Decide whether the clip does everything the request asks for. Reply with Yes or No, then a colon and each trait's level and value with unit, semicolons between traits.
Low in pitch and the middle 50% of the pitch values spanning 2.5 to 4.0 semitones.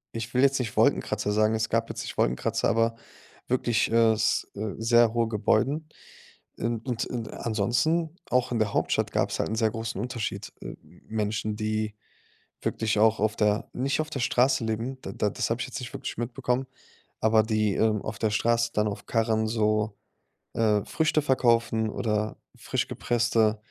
No: low, 115 Hz; narrow, 1.9 semitones